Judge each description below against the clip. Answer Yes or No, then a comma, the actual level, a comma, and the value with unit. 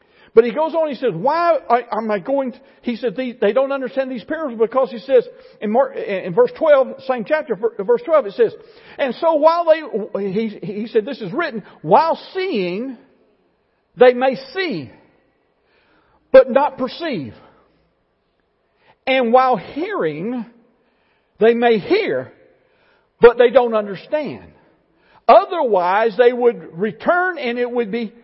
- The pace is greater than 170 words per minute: No, average, 145 wpm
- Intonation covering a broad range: Yes, wide, 5.8 semitones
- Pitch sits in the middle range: No, very high, 260 Hz